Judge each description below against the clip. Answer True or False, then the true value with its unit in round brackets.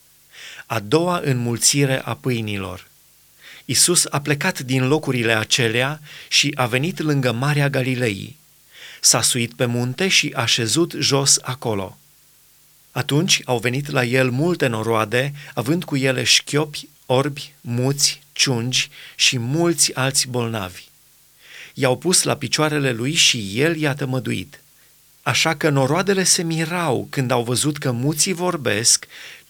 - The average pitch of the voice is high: False (140 Hz)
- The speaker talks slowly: False (130 wpm)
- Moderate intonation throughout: True (3.3 semitones)